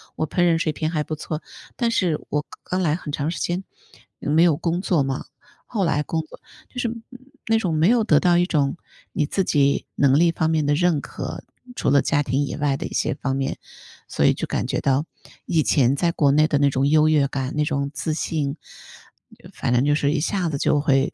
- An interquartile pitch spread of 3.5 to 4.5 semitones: No, average, 3.0 semitones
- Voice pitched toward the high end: No, medium, 150 Hz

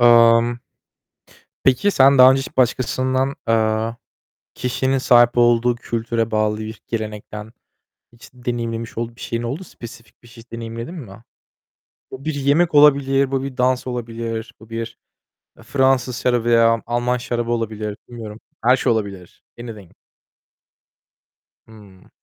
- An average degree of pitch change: No, narrow, 2.3 semitones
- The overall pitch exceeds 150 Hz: No, low, 120 Hz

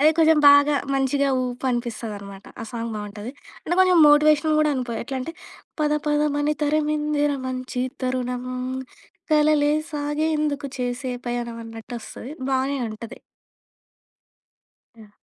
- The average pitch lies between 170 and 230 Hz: No, very high, 270 Hz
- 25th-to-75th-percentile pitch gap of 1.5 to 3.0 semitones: No, average, 3.6 semitones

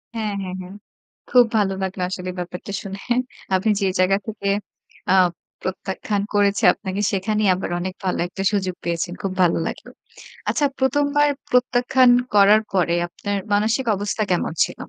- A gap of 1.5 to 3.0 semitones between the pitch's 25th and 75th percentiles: Yes, average, 2.7 semitones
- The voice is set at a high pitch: Yes, high, 200 Hz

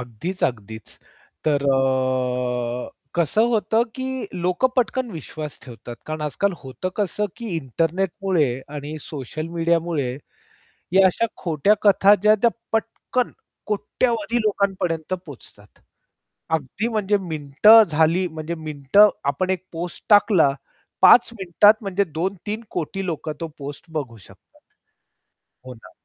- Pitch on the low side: No, medium, 170 Hz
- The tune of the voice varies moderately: No, wide, 6.3 semitones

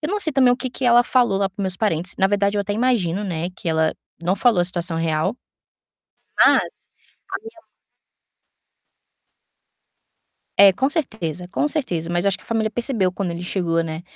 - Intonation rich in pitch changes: Yes, wide, 5.7 semitones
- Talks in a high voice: Yes, high, 195 Hz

